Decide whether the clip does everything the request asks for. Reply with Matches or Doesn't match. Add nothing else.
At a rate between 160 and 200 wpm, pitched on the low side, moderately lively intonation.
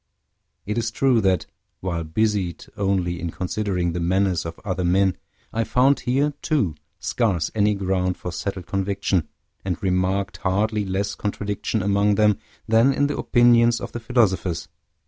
Doesn't match